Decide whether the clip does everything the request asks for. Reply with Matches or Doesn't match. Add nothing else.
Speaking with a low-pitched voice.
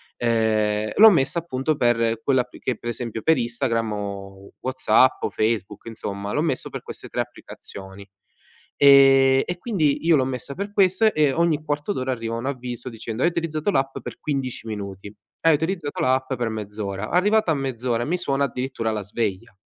Matches